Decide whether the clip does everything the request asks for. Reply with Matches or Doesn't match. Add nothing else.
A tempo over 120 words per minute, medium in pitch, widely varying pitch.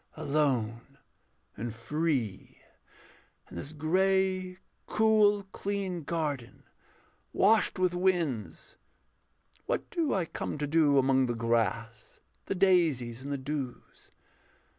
Doesn't match